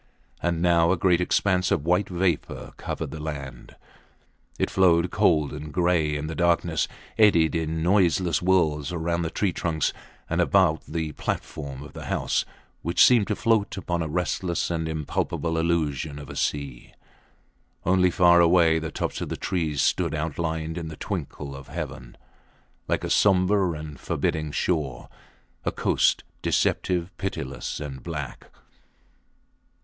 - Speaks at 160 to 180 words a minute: No, average, 150 wpm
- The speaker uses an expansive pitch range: No, average, 2.7 semitones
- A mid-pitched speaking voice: No, very low, 85 Hz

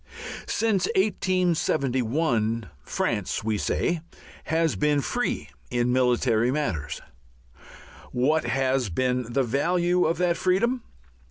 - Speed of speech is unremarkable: No, slow, 100 wpm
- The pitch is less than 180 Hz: Yes, medium, 140 Hz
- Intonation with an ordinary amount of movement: No, wide, 6.3 semitones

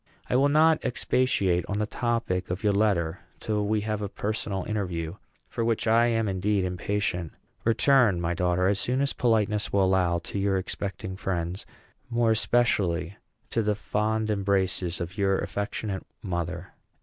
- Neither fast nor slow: Yes, average, 160 wpm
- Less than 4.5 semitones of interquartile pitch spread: Yes, average, 3.2 semitones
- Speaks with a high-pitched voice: No, low, 100 Hz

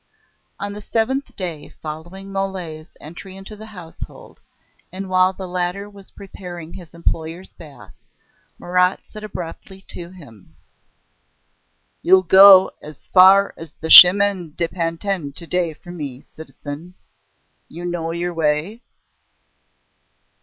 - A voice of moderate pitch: Yes, medium, 180 Hz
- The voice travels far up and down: No, average, 2.9 semitones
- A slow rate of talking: Yes, slow, 125 wpm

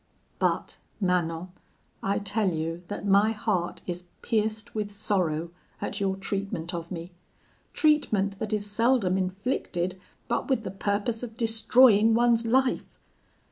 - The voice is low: No, high, 205 Hz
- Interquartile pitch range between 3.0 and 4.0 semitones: Yes, average, 3.5 semitones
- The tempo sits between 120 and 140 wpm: Yes, slow, 135 wpm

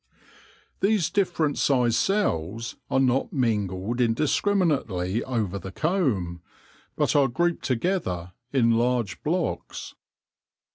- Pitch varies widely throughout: Yes, wide, 7.8 semitones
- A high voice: No, low, 125 Hz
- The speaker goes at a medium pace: No, slow, 105 wpm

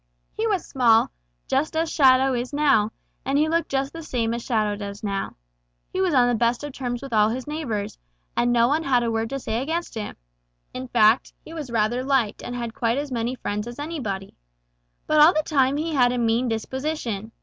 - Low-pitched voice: No, very high, 250 Hz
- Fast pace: Yes, fast, 215 wpm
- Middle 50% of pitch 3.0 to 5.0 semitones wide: Yes, average, 4.3 semitones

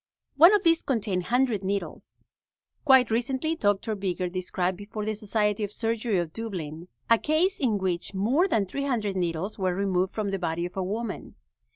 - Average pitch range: Yes, average, 4.2 semitones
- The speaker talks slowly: No, average, 175 wpm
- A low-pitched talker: No, high, 205 Hz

